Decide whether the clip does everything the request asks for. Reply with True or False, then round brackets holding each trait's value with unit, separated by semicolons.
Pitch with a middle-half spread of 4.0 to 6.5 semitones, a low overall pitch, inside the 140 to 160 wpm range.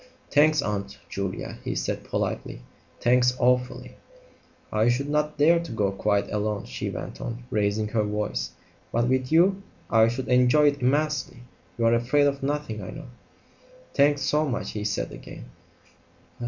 True (5.3 semitones; 125 Hz; 155 wpm)